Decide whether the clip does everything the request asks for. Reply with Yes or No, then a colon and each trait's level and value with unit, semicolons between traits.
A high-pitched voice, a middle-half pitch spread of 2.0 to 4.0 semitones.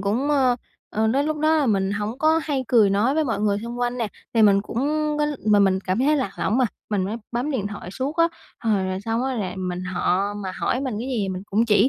No: high, 220 Hz; average, 4.8 semitones